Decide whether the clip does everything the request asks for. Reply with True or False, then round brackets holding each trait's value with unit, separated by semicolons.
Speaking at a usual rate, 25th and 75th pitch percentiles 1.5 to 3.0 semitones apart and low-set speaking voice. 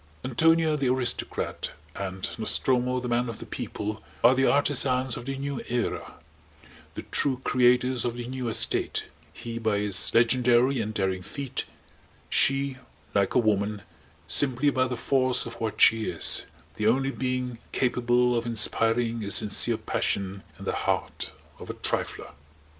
True (155 wpm; 2.6 semitones; 120 Hz)